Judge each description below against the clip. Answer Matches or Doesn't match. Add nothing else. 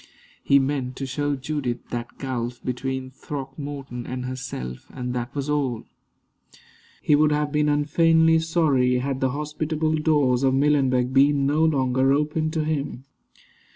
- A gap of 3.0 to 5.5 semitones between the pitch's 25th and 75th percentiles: Doesn't match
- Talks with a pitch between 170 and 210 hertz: Doesn't match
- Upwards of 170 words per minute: Doesn't match